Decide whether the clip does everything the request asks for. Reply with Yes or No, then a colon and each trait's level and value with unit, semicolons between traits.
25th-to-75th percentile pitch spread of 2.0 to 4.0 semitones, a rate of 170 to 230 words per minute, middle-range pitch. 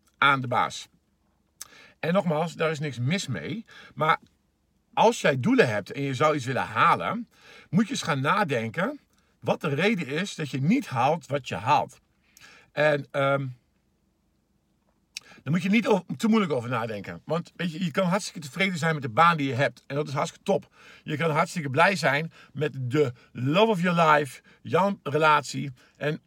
No: average, 5.1 semitones; average, 185 wpm; medium, 155 Hz